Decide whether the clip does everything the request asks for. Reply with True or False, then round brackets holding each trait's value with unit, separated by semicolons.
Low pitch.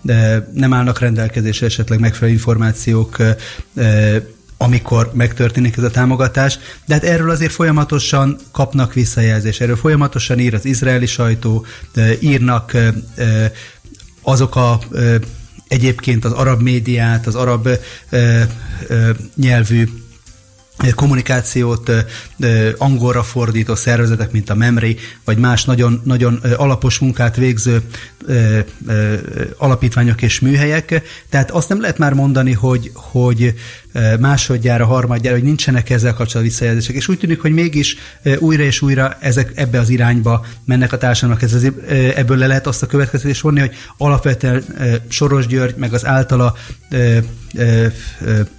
True (120 Hz)